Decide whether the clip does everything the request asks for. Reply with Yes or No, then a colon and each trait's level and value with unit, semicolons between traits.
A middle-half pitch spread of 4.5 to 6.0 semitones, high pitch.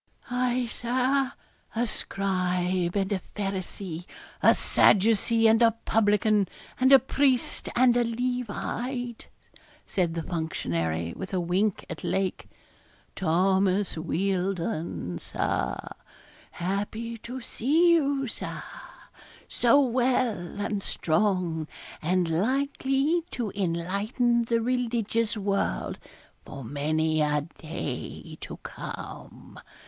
Yes: wide, 5.5 semitones; high, 205 Hz